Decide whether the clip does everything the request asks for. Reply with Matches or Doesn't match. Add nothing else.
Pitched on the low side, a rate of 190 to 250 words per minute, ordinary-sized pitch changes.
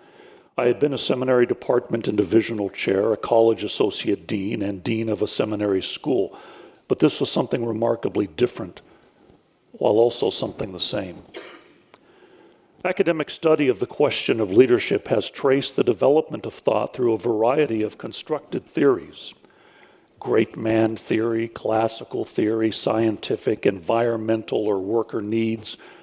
Doesn't match